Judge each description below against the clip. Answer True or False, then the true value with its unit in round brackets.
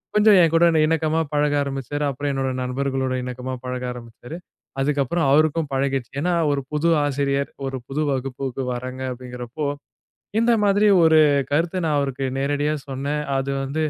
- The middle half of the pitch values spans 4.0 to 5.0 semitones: False (2.8 semitones)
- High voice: False (140 Hz)